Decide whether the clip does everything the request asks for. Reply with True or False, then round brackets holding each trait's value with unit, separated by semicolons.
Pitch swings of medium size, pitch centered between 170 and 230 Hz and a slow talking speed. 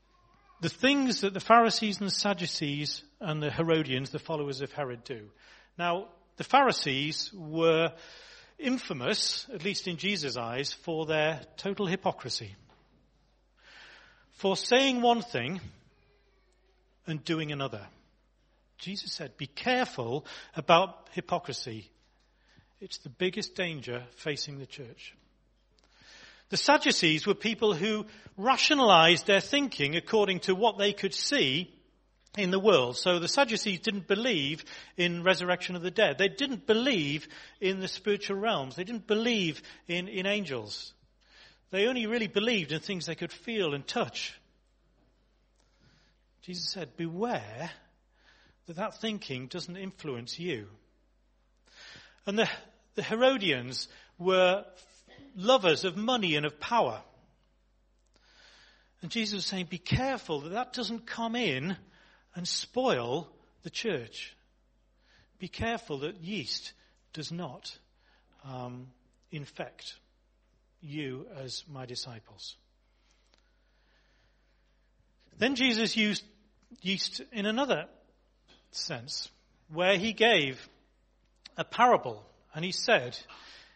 False (5.9 semitones; 185 Hz; 115 wpm)